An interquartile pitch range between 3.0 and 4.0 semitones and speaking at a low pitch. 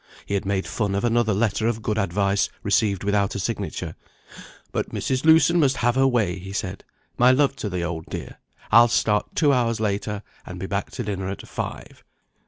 Yes: average, 3.5 semitones; low, 105 Hz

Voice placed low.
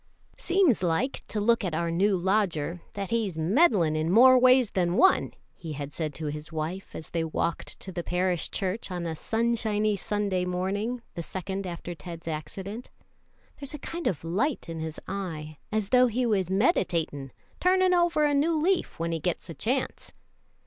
No: high, 190 Hz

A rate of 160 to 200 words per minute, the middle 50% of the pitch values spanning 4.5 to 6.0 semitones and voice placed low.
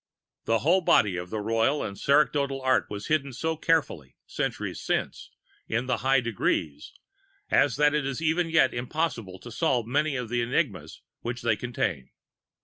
Yes: average, 165 wpm; average, 4.8 semitones; low, 125 Hz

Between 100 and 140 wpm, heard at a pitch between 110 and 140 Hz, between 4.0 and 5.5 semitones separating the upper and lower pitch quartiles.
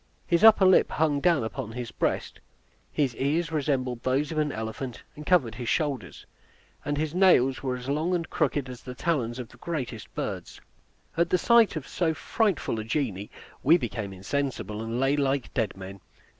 No: average, 185 wpm; low, 135 Hz; average, 5.1 semitones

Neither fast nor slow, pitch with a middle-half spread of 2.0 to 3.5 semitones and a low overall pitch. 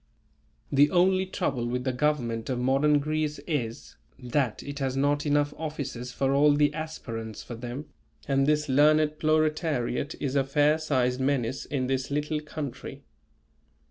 No: average, 150 wpm; average, 2.8 semitones; medium, 145 Hz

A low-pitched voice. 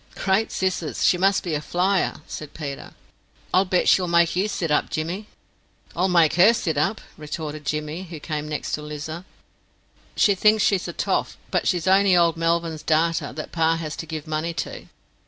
No: medium, 165 Hz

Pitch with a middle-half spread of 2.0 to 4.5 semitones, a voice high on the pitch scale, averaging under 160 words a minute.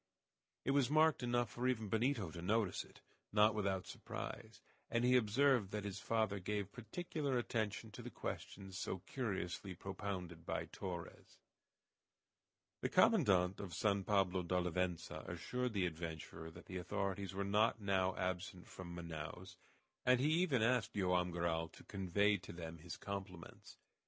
No: average, 3.8 semitones; low, 100 Hz; average, 150 wpm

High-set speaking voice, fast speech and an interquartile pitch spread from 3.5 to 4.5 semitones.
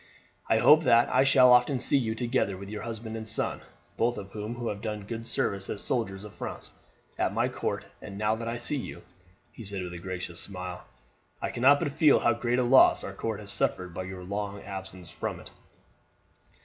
No: low, 110 Hz; fast, 210 wpm; average, 3.8 semitones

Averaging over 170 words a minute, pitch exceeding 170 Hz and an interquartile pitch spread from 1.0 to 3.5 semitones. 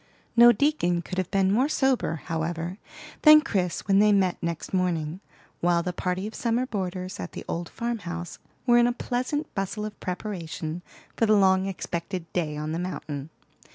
No: average, 180 wpm; medium, 185 Hz; average, 4.3 semitones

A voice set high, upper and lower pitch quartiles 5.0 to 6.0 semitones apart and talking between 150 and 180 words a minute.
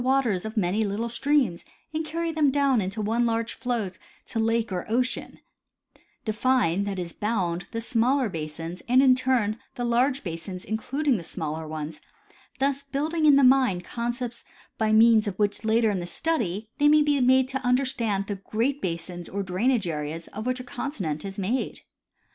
Yes: high, 230 Hz; wide, 5.4 semitones; average, 175 wpm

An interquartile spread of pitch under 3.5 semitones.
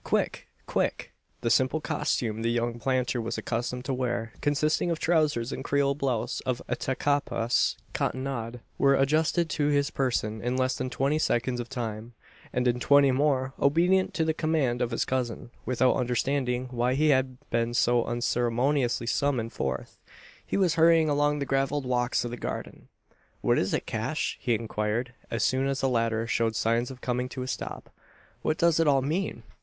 Yes: average, 3.0 semitones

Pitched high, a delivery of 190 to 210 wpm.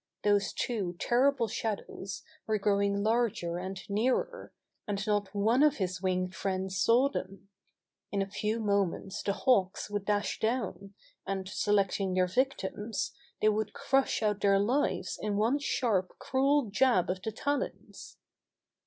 No: high, 205 Hz; average, 145 wpm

